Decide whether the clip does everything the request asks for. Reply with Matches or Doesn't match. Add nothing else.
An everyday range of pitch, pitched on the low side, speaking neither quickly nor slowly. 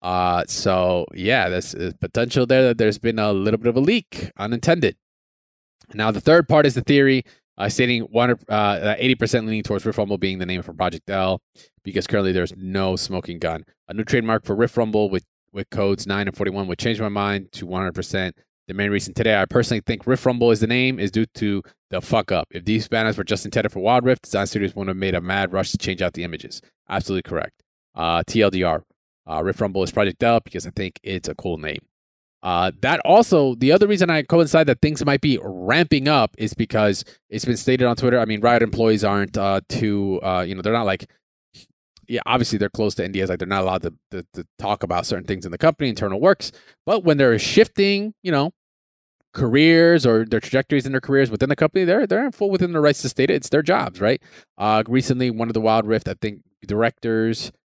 Doesn't match